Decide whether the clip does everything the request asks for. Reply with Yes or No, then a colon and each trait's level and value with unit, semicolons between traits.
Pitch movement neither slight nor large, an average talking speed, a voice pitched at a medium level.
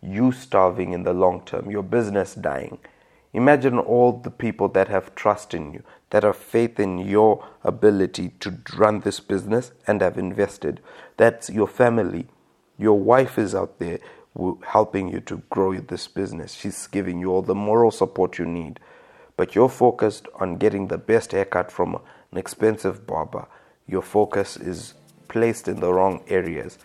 No: average, 4.0 semitones; average, 165 wpm; low, 105 Hz